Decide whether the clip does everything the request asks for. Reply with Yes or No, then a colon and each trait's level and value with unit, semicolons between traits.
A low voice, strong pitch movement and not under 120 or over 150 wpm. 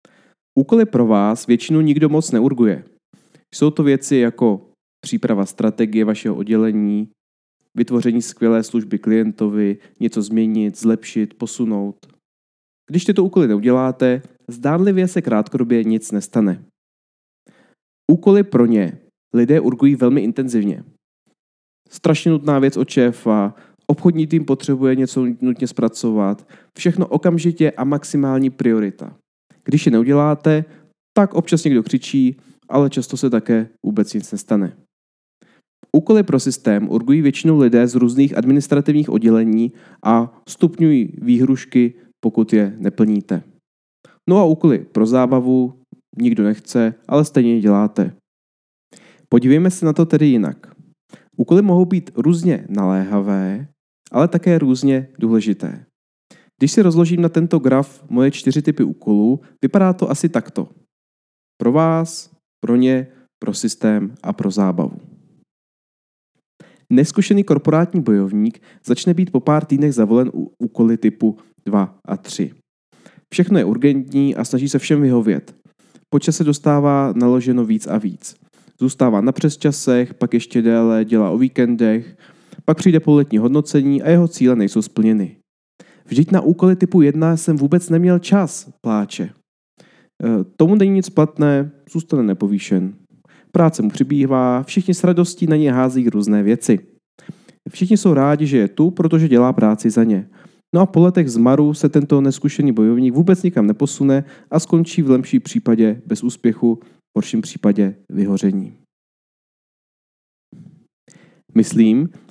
Yes: low, 130 Hz; wide, 6.0 semitones; average, 130 wpm